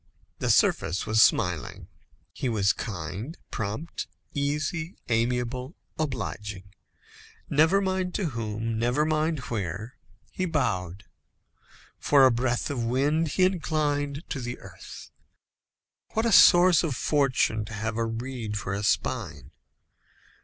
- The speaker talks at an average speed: No, slow, 125 wpm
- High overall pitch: No, low, 125 Hz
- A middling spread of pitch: No, wide, 5.9 semitones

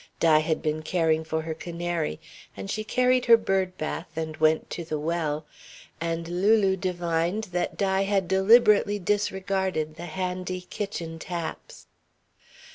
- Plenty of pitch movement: No, average, 3.1 semitones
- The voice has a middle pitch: Yes, medium, 175 Hz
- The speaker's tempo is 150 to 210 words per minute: No, average, 140 wpm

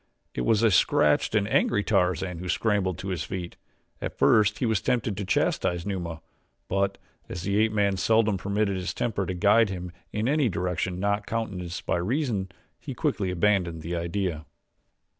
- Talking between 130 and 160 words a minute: No, average, 175 wpm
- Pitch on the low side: Yes, very low, 95 Hz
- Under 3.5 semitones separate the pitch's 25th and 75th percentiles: Yes, average, 2.9 semitones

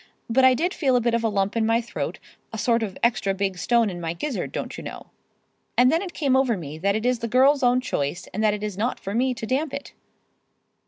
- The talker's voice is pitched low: No, high, 230 Hz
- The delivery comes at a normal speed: No, fast, 260 wpm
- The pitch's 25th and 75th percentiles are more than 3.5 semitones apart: Yes, average, 4.2 semitones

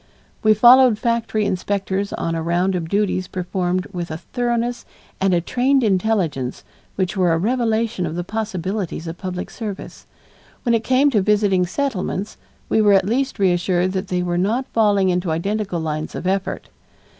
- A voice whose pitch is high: Yes, high, 195 Hz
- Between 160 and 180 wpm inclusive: Yes, average, 165 wpm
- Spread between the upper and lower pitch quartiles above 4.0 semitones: No, average, 3.6 semitones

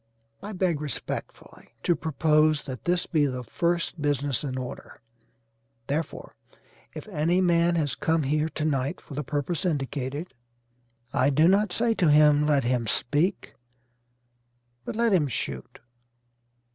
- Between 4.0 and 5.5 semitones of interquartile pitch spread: No, average, 3.4 semitones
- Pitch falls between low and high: Yes, medium, 150 Hz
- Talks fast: No, average, 140 wpm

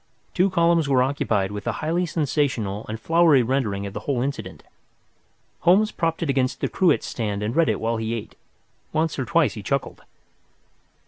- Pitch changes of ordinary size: No, wide, 6.8 semitones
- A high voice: No, low, 135 Hz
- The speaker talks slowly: No, average, 180 wpm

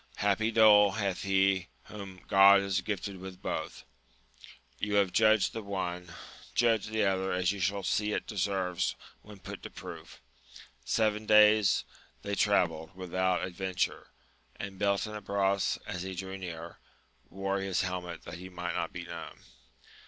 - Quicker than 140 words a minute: Yes, average, 150 wpm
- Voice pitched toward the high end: No, very low, 95 Hz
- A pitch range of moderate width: No, narrow, 2.0 semitones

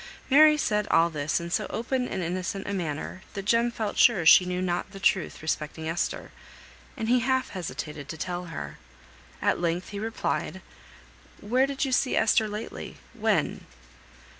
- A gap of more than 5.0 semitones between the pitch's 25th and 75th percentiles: Yes, wide, 5.4 semitones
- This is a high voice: Yes, high, 195 Hz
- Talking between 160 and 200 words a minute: Yes, average, 165 wpm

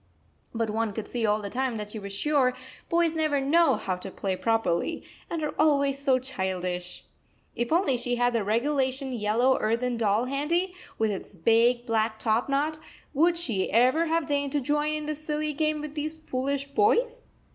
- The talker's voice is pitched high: Yes, very high, 260 Hz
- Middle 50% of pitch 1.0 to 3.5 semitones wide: No, average, 5.3 semitones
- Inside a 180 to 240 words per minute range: Yes, average, 185 wpm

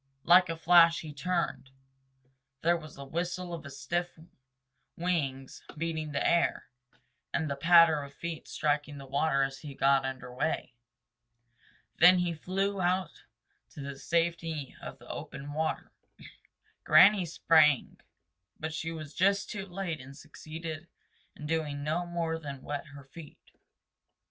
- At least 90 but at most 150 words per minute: Yes, average, 140 wpm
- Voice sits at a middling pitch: Yes, medium, 160 Hz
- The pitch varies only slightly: No, average, 3.3 semitones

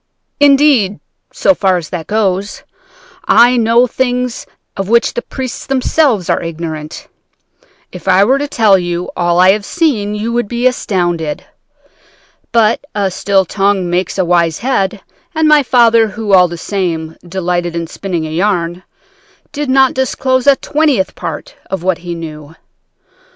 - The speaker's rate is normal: Yes, average, 155 wpm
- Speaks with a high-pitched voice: Yes, high, 200 Hz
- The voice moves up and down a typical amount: No, wide, 5.9 semitones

